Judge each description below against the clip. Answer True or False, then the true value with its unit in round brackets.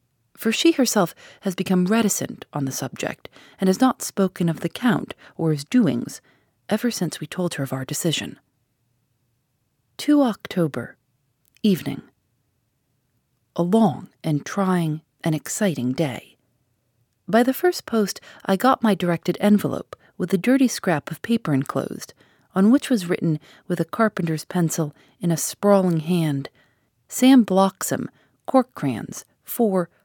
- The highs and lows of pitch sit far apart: True (7.3 semitones)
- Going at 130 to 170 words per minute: True (140 wpm)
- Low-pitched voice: False (170 Hz)